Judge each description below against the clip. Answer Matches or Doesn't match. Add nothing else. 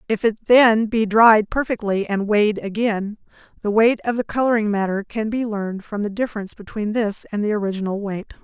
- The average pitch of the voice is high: Matches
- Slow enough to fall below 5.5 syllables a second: Doesn't match